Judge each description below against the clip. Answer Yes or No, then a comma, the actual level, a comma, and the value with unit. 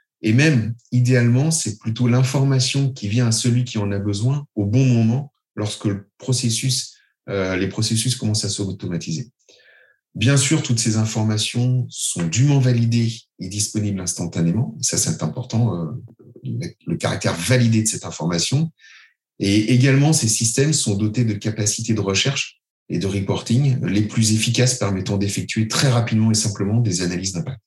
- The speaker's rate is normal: Yes, average, 155 wpm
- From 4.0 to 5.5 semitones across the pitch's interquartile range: No, average, 3.4 semitones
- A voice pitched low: Yes, low, 115 Hz